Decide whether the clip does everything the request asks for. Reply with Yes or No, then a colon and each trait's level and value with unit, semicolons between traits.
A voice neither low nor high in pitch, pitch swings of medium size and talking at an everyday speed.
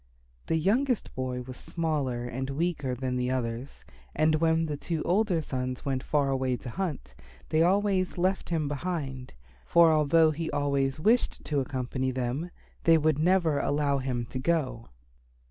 Yes: medium, 145 Hz; average, 4.2 semitones; average, 160 wpm